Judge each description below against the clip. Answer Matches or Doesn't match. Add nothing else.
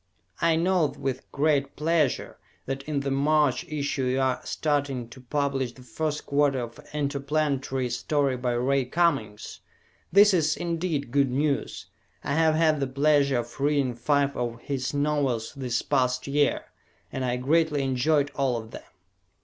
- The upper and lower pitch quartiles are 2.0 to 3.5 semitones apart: Matches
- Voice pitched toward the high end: Doesn't match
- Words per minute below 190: Matches